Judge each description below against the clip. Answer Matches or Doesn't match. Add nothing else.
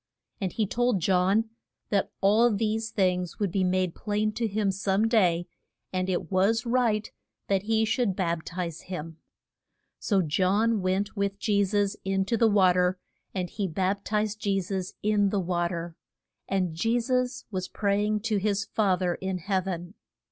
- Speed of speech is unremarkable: Matches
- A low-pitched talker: Doesn't match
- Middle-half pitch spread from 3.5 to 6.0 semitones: Doesn't match